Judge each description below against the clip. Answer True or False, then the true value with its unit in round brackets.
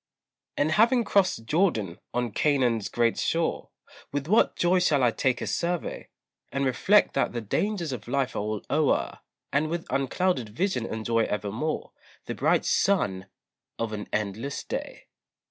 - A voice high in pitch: False (140 Hz)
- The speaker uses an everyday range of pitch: False (7.3 semitones)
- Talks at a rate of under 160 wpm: True (150 wpm)